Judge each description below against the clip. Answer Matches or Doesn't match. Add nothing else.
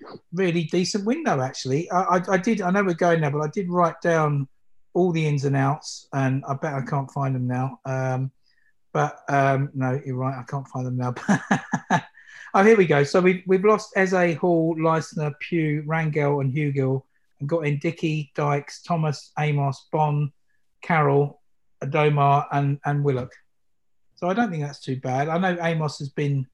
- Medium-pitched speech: Matches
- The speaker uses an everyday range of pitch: Matches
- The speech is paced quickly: Doesn't match